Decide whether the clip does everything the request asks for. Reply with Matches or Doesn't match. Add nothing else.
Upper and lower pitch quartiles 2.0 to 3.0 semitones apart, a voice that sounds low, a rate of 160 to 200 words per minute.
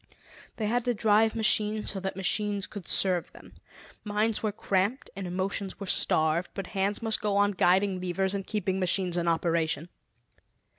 Doesn't match